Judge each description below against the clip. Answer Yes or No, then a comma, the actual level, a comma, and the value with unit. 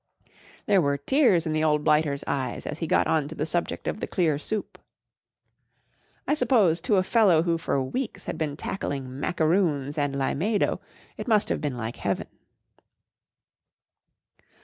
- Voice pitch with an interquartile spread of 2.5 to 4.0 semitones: No, average, 5.2 semitones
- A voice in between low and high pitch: Yes, medium, 160 Hz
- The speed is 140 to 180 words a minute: Yes, average, 155 wpm